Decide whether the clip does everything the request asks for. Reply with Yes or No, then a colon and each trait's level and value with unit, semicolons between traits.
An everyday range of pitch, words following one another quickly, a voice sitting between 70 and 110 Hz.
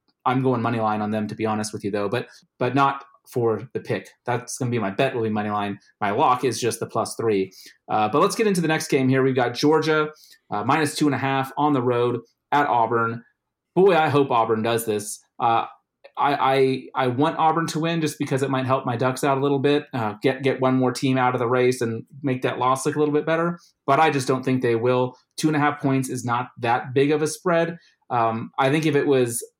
No: average, 3.4 semitones; fast, 255 wpm; low, 130 Hz